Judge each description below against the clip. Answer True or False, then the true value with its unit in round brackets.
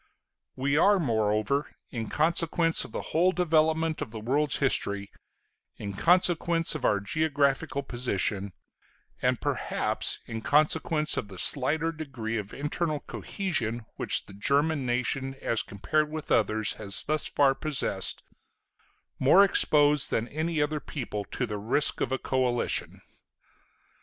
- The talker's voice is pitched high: False (140 Hz)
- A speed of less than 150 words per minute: True (135 wpm)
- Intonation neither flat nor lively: False (5.8 semitones)